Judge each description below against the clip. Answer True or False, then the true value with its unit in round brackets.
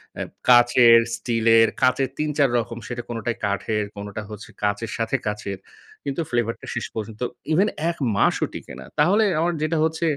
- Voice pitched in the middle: False (120 Hz)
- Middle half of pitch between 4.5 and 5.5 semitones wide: True (4.8 semitones)